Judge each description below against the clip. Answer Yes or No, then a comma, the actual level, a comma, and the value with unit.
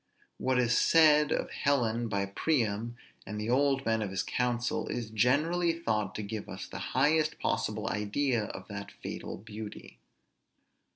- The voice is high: No, low, 120 Hz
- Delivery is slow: No, average, 155 wpm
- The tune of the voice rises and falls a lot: No, average, 4.9 semitones